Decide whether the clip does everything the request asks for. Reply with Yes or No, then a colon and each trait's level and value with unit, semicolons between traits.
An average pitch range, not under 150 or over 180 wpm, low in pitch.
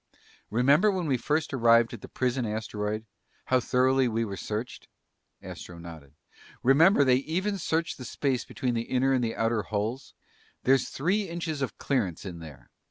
Yes: average, 4.4 semitones; average, 165 wpm; low, 125 Hz